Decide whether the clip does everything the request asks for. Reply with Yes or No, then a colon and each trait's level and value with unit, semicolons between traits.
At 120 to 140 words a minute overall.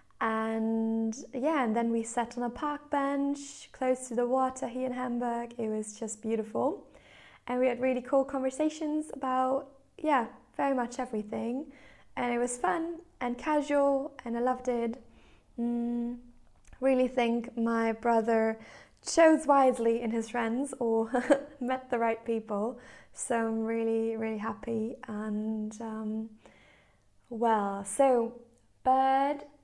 Yes: slow, 135 wpm